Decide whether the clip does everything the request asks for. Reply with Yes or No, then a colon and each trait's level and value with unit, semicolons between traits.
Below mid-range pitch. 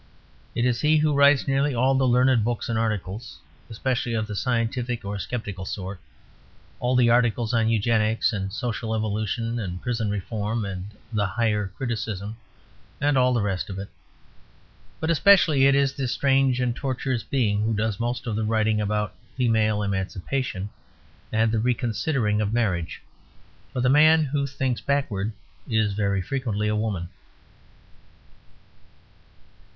Yes: low, 115 Hz